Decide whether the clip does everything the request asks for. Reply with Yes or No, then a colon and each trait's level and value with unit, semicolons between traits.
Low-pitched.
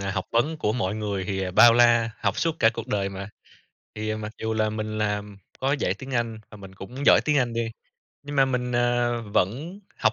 Yes: low, 110 Hz